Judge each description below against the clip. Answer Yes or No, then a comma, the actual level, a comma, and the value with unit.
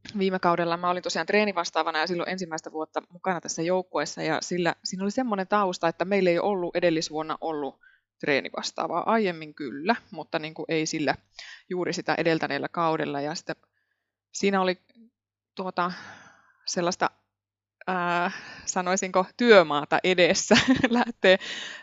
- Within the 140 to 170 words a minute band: No, average, 130 wpm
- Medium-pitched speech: Yes, medium, 175 Hz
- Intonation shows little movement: No, average, 3.2 semitones